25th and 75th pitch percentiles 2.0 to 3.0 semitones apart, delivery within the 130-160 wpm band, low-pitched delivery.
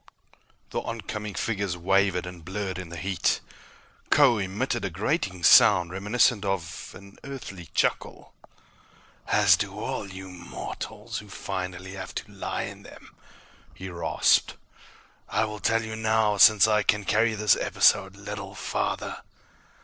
Yes: narrow, 2.5 semitones; average, 140 wpm; low, 100 Hz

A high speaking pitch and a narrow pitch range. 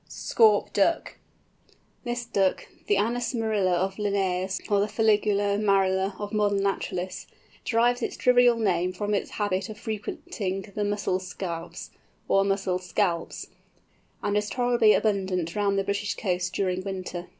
Yes: high, 200 Hz; narrow, 2.1 semitones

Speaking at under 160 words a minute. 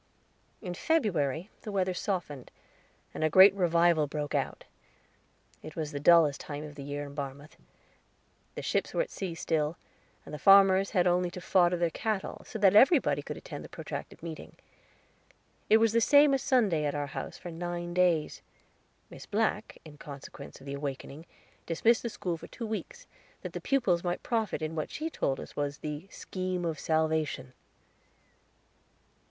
No: average, 170 wpm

